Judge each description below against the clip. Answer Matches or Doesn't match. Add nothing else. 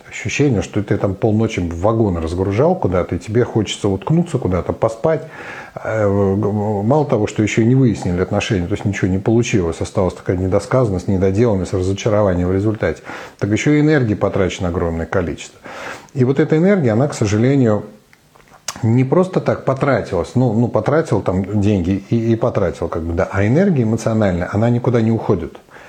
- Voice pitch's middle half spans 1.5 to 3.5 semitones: Doesn't match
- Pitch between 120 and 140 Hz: Doesn't match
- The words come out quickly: Matches